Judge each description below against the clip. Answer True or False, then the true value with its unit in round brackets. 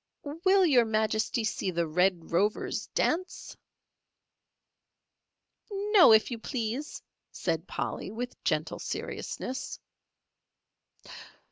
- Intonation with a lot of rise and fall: True (7.4 semitones)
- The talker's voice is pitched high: True (225 Hz)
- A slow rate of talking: True (90 wpm)